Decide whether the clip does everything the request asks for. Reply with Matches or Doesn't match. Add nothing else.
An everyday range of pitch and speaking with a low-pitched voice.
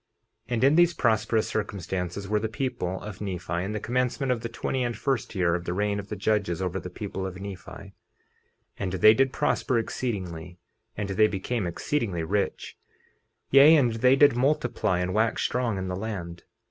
Matches